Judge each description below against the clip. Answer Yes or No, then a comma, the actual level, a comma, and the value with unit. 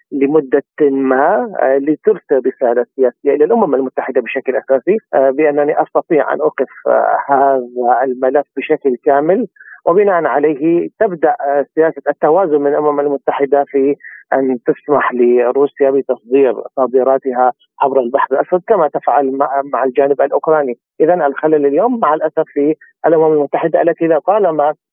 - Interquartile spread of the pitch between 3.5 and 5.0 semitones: No, average, 2.8 semitones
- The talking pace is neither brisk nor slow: Yes, average, 120 wpm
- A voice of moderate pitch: Yes, medium, 145 Hz